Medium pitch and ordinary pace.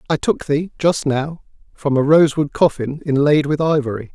Yes: medium, 145 Hz; average, 190 wpm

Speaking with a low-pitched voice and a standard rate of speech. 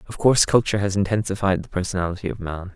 Yes: very low, 95 Hz; average, 195 wpm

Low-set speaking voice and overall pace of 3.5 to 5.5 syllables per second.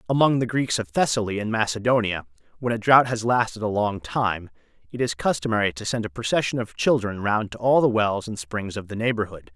No: low, 110 Hz; 5.7 syllables/s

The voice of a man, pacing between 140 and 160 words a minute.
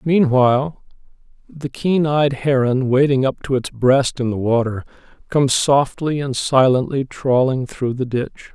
Yes: male; average, 145 wpm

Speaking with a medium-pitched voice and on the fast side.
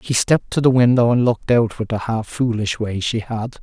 No: low, 115 Hz; fast, 250 wpm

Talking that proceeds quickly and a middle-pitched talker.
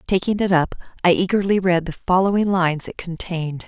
No: average, 180 wpm; medium, 180 Hz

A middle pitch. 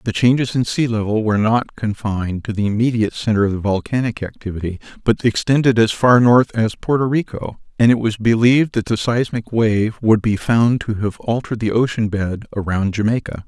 No: low, 110 Hz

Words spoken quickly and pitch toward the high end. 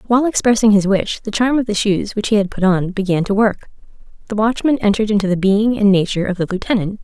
Yes: fast, 240 wpm; high, 205 Hz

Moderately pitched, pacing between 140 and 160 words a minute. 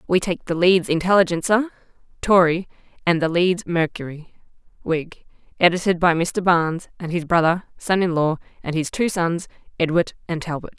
Yes: medium, 175 Hz; average, 155 wpm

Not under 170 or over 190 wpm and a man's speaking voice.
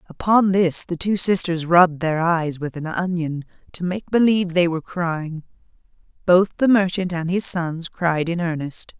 No: average, 175 wpm; female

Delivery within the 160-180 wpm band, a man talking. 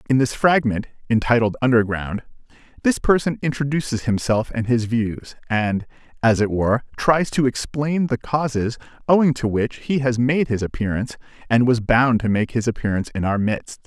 Yes: average, 170 wpm; male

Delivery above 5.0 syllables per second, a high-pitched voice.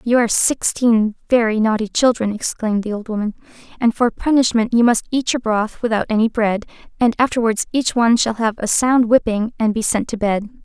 Yes: 5.5 syllables/s; high, 225 Hz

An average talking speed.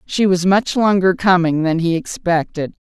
Yes: average, 165 wpm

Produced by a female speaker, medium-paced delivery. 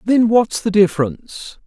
No: male; average, 145 wpm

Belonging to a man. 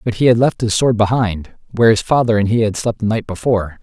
Yes: male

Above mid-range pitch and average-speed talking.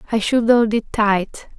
Yes: high, 220 Hz; average, 190 wpm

